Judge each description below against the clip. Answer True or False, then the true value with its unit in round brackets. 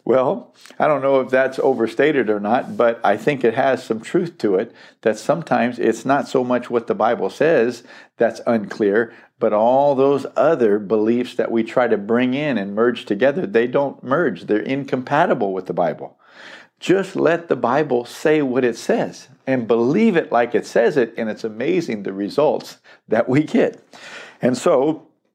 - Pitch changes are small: False (3.2 semitones)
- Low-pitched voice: True (125 Hz)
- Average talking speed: True (180 wpm)